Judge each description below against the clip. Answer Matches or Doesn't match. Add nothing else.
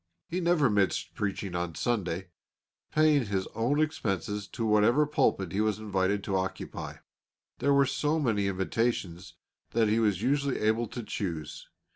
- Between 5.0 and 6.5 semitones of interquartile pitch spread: Matches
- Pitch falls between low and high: Doesn't match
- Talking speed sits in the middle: Matches